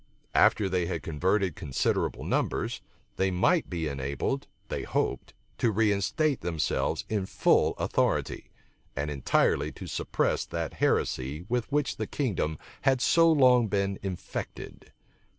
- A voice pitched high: No, very low, 95 Hz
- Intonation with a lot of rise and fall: Yes, wide, 7.2 semitones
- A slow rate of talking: Yes, slow, 130 wpm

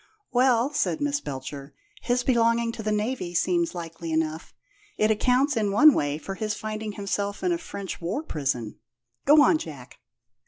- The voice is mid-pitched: No, high, 210 Hz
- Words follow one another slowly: No, average, 165 wpm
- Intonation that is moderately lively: No, wide, 7.1 semitones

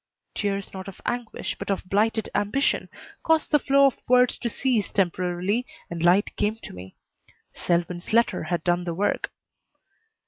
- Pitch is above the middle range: Yes, high, 200 Hz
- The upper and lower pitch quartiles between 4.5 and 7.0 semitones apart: Yes, average, 5.1 semitones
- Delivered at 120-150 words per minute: No, average, 160 wpm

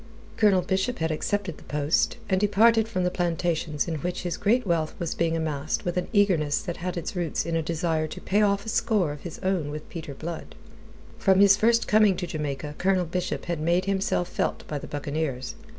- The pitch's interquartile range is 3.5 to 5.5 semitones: Yes, average, 3.8 semitones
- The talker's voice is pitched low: No, medium, 175 Hz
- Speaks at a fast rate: Yes, fast, 210 wpm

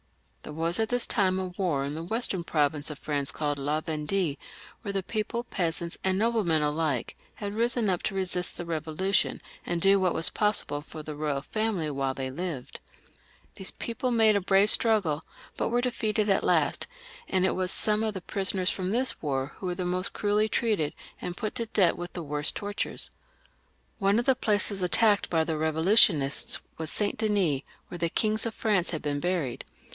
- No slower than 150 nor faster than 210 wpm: Yes, average, 190 wpm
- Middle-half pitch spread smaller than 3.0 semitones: No, average, 5.1 semitones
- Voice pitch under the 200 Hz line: Yes, medium, 185 Hz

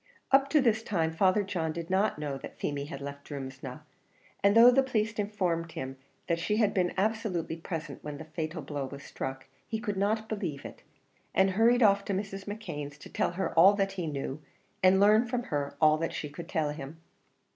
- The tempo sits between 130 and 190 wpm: No, fast, 205 wpm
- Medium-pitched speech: Yes, medium, 180 Hz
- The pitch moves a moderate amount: No, wide, 5.7 semitones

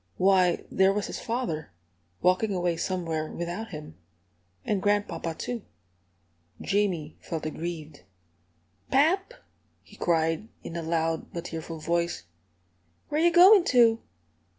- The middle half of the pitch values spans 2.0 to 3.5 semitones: No, average, 5.1 semitones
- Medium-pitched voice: Yes, medium, 175 Hz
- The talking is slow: Yes, slow, 120 wpm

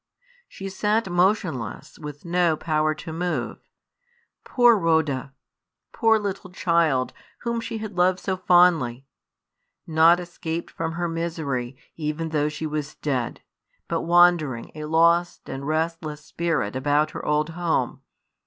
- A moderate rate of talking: No, slow, 130 wpm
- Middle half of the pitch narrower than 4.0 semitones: Yes, average, 2.8 semitones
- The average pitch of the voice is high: No, medium, 165 Hz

